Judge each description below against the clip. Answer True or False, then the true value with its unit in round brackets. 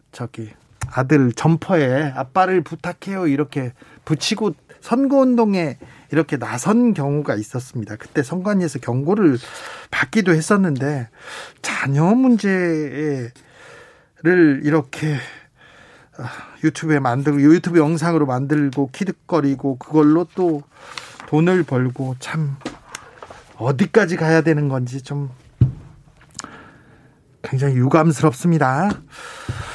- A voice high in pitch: False (150 Hz)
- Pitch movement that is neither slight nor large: True (4.3 semitones)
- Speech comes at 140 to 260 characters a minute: True (230 characters per minute)